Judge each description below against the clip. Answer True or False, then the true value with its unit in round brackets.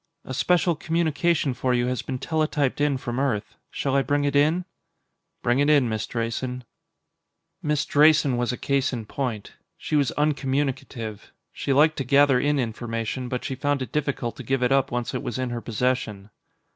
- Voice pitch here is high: False (135 Hz)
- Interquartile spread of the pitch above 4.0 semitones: False (2.9 semitones)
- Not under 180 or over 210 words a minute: True (185 wpm)